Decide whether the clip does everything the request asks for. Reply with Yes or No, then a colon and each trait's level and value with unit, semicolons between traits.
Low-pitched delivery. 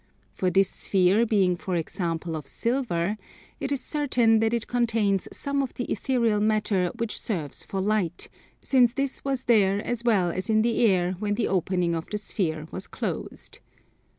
No: high, 210 Hz